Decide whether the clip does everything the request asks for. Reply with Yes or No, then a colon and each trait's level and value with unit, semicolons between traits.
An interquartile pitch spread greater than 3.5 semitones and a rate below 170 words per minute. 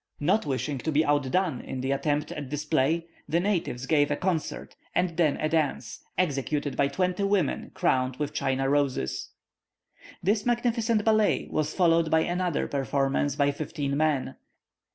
Yes: average, 4.2 semitones; average, 155 wpm